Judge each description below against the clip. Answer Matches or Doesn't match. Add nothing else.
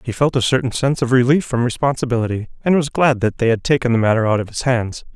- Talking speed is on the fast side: Matches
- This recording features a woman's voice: Doesn't match